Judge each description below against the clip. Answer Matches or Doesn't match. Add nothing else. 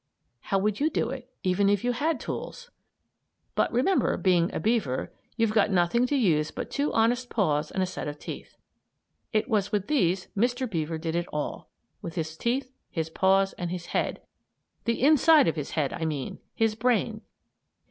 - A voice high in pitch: Matches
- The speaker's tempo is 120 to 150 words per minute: Doesn't match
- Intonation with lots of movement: Matches